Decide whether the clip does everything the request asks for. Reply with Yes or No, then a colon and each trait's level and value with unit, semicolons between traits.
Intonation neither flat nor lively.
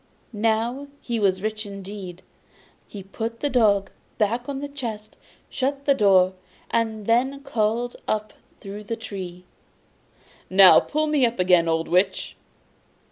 Yes: average, 3.7 semitones